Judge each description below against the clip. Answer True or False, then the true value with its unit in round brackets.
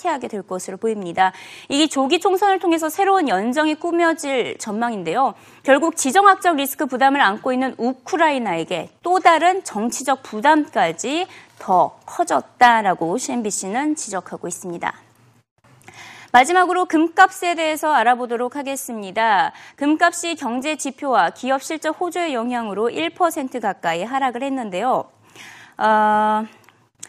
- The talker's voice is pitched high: True (275 Hz)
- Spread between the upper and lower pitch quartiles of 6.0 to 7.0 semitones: True (6.7 semitones)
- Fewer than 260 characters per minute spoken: False (305 characters per minute)